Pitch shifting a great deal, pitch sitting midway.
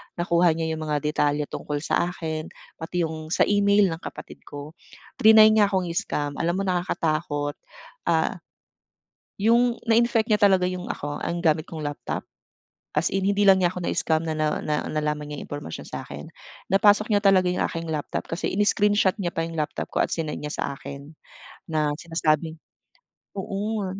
No: average, 4.4 semitones; medium, 170 Hz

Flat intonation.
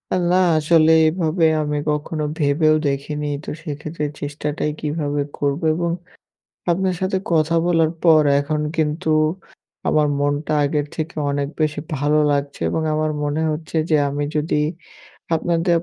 Yes: narrow, 1.9 semitones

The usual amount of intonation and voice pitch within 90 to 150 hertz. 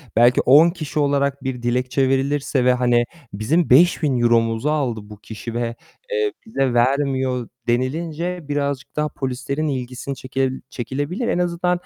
Yes: average, 3.5 semitones; low, 135 Hz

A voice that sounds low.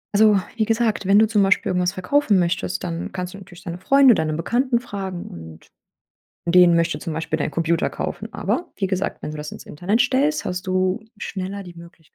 No: medium, 185 Hz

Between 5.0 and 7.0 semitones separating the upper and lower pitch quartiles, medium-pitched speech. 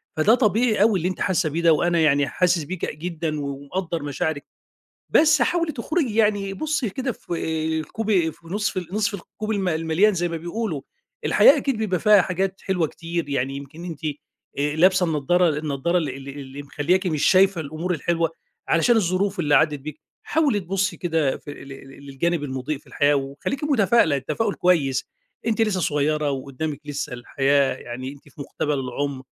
Yes: average, 5.3 semitones; medium, 165 Hz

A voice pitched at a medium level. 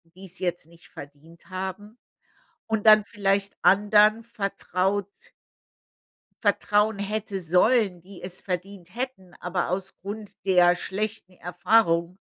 No: high, 195 Hz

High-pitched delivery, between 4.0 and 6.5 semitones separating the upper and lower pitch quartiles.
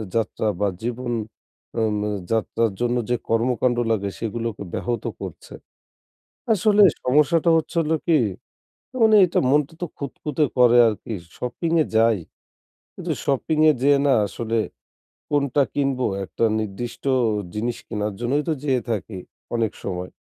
No: low, 120 Hz; average, 4.3 semitones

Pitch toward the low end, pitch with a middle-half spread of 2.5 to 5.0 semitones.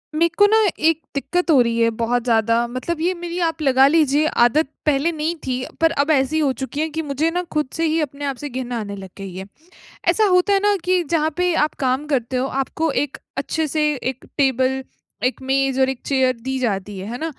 No: very high, 280 Hz; average, 4.0 semitones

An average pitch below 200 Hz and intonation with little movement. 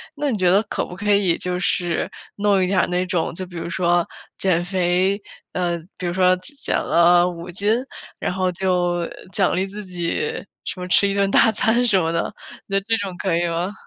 Yes: medium, 185 Hz; narrow, 2.2 semitones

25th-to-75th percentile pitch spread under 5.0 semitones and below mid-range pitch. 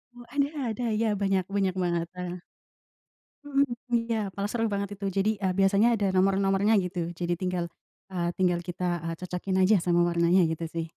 No: narrow, 2.5 semitones; medium, 185 Hz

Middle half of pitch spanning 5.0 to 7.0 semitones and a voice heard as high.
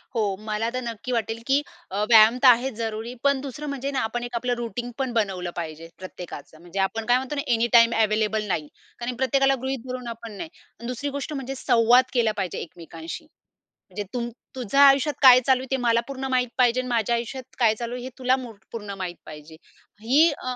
No: average, 3.1 semitones; high, 240 Hz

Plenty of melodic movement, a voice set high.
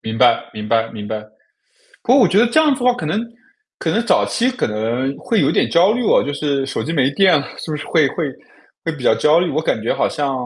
No: wide, 9.0 semitones; medium, 150 Hz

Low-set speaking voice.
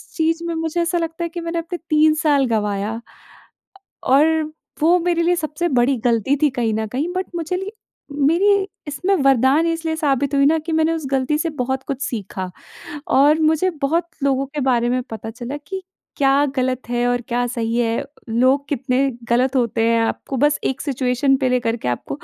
No: very high, 275 Hz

